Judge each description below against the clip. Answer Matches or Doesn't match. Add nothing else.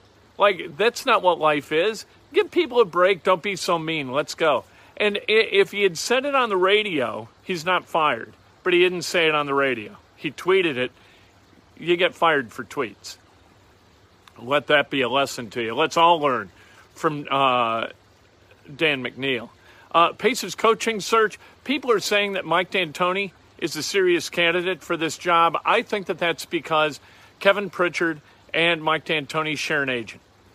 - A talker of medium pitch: Matches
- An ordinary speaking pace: Matches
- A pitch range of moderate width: Doesn't match